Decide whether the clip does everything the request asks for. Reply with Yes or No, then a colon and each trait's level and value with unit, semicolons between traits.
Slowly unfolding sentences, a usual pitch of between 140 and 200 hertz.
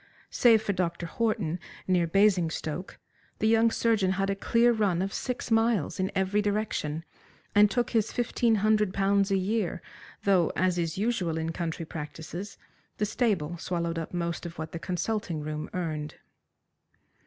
No: average, 155 wpm; high, 190 Hz